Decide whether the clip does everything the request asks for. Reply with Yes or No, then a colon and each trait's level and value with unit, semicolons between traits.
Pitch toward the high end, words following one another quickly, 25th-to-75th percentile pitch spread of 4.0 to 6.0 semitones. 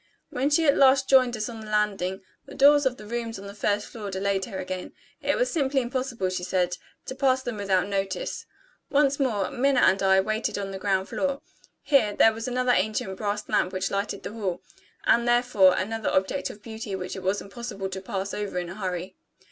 Yes: high, 210 Hz; fast, 210 wpm; average, 4.6 semitones